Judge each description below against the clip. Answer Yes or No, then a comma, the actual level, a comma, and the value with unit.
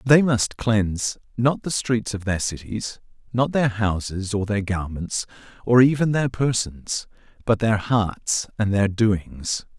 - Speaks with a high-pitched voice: No, low, 110 Hz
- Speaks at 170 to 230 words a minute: No, average, 155 wpm